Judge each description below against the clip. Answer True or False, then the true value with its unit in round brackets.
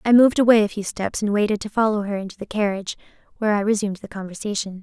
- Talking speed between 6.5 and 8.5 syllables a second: True (7.4 syllables/s)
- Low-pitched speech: False (205 Hz)